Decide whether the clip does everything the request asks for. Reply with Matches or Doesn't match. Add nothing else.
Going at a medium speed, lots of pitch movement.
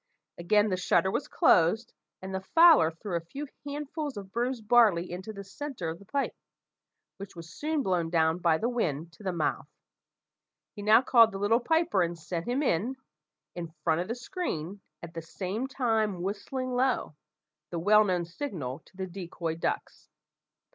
Matches